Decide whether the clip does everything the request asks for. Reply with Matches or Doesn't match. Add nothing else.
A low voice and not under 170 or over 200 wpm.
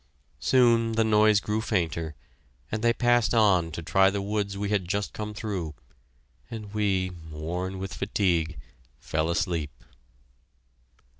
Doesn't match